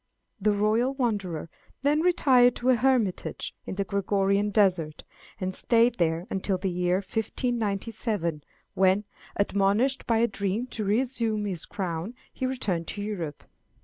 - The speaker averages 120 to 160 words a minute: Yes, average, 140 wpm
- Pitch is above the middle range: Yes, high, 205 Hz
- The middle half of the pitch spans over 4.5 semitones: No, average, 4.0 semitones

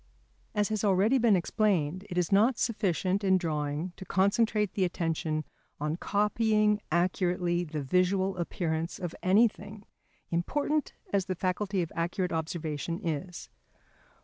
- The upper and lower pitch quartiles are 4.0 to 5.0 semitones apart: No, average, 3.5 semitones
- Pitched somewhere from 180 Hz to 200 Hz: Yes, medium, 185 Hz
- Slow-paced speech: Yes, slow, 130 wpm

